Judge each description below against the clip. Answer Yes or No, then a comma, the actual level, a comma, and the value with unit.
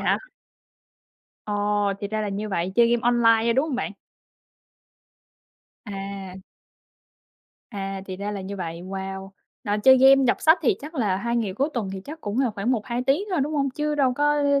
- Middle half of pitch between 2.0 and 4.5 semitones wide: No, average, 5.2 semitones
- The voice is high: Yes, high, 220 Hz